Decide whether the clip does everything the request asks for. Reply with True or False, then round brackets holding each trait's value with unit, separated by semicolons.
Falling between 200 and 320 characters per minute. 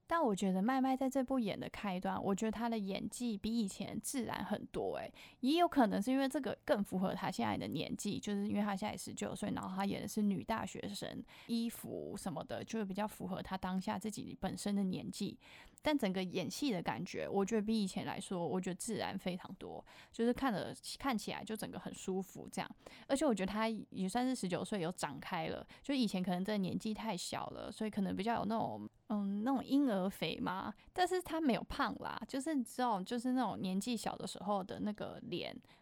False (330 characters per minute)